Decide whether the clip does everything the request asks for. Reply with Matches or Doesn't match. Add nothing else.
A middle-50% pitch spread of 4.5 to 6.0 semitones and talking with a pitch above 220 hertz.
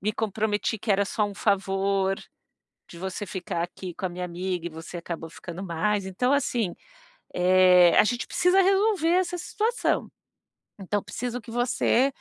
Doesn't match